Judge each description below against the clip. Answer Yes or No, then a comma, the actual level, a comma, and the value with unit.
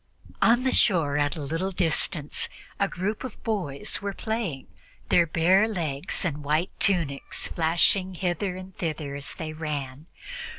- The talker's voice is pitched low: No, medium, 170 Hz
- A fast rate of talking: No, average, 145 wpm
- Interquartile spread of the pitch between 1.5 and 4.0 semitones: No, average, 4.5 semitones